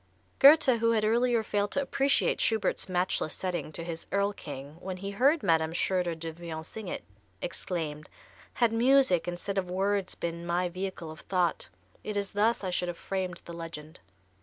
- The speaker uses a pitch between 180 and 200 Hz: Yes, medium, 185 Hz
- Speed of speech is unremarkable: Yes, average, 175 wpm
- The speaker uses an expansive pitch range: No, average, 4.0 semitones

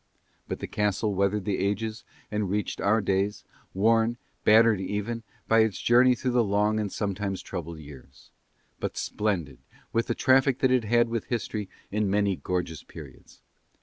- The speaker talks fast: No, average, 160 wpm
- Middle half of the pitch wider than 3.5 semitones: No, average, 2.8 semitones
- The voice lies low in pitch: Yes, low, 105 Hz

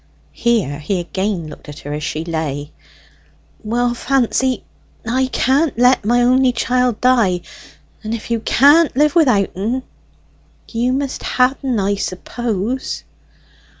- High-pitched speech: Yes, high, 235 Hz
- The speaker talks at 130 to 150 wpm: Yes, slow, 135 wpm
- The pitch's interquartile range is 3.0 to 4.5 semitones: No, average, 5.1 semitones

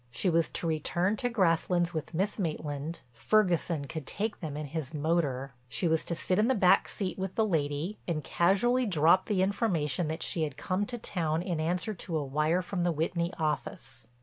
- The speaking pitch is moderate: Yes, medium, 170 Hz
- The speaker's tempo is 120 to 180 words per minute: No, average, 200 wpm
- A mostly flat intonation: No, average, 3.5 semitones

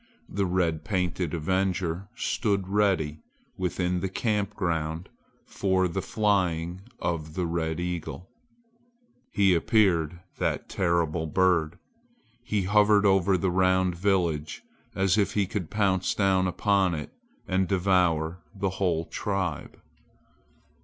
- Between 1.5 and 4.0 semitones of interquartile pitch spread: Yes, narrow, 2.4 semitones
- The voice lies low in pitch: Yes, very low, 95 Hz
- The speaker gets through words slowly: Yes, slow, 120 wpm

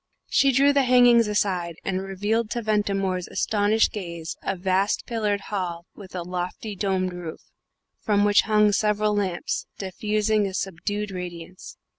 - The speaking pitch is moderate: No, high, 200 Hz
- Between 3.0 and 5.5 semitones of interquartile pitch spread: No, narrow, 2.5 semitones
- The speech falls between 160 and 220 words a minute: No, average, 145 wpm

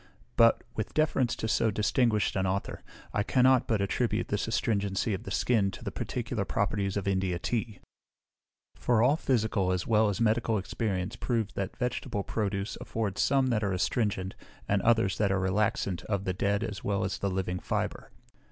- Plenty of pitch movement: No, average, 2.8 semitones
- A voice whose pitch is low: Yes, low, 105 Hz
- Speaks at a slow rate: No, average, 180 wpm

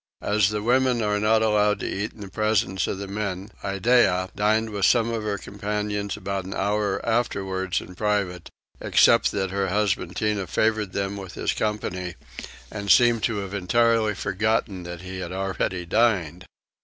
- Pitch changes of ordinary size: No, narrow, 2.2 semitones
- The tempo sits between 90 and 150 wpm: No, average, 170 wpm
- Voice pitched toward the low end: Yes, low, 100 Hz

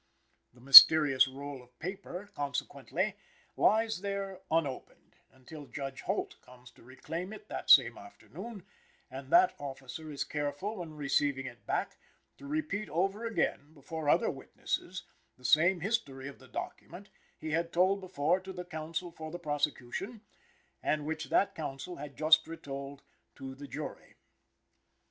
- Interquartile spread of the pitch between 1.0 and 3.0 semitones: No, average, 5.1 semitones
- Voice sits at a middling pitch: Yes, medium, 155 Hz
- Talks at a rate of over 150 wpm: No, average, 145 wpm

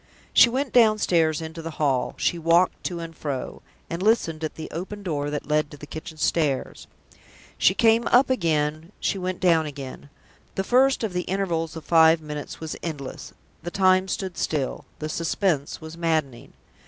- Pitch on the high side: No, medium, 165 Hz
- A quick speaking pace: No, average, 175 wpm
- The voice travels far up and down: No, average, 3.5 semitones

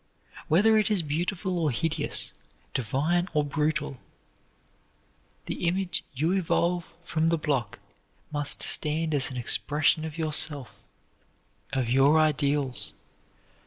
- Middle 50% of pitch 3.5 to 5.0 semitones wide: No, average, 3.0 semitones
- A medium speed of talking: No, slow, 115 wpm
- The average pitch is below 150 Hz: No, medium, 155 Hz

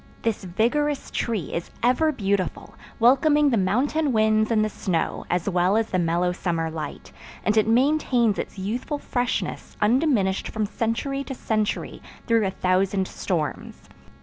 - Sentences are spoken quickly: No, average, 150 wpm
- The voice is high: Yes, high, 215 Hz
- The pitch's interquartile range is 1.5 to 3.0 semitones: No, average, 4.9 semitones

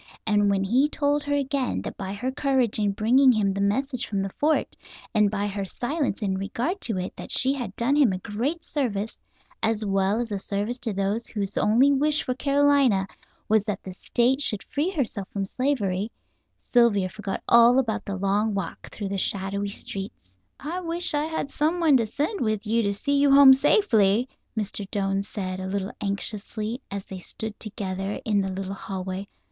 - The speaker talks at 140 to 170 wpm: No, average, 195 wpm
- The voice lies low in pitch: No, high, 215 Hz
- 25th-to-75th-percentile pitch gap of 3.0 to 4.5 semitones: No, average, 5.2 semitones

